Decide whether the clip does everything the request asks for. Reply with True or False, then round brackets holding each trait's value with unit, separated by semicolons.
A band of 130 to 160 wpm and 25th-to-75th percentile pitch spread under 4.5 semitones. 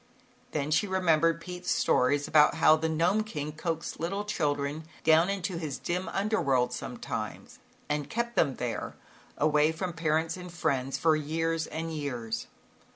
True (155 wpm; 3.0 semitones)